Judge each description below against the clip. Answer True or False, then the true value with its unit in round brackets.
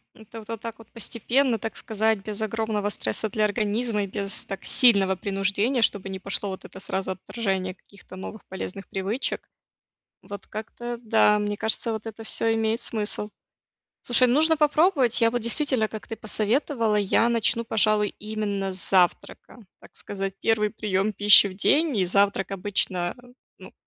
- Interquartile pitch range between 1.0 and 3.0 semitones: True (2.6 semitones)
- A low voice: False (215 Hz)